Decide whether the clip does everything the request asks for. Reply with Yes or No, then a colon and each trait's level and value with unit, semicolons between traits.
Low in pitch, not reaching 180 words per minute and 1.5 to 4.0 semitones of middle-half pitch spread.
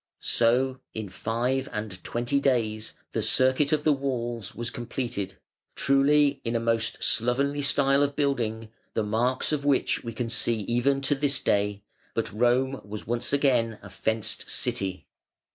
Yes: low, 120 Hz; average, 155 wpm; average, 3.6 semitones